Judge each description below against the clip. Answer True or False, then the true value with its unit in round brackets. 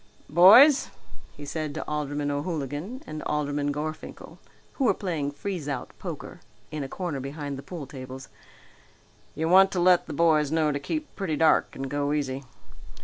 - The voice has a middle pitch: True (150 Hz)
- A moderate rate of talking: True (165 wpm)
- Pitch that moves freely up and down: False (3.3 semitones)